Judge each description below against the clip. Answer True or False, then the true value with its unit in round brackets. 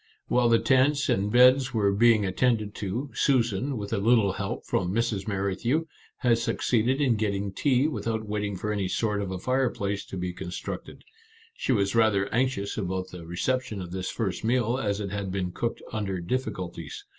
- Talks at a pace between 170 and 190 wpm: True (180 wpm)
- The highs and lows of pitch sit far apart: False (3.8 semitones)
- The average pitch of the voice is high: False (105 Hz)